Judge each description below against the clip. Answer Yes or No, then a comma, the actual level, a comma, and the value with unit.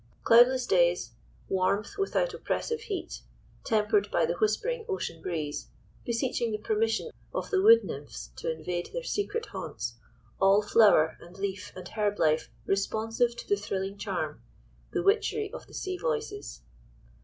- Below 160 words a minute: Yes, average, 145 wpm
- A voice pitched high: Yes, high, 215 Hz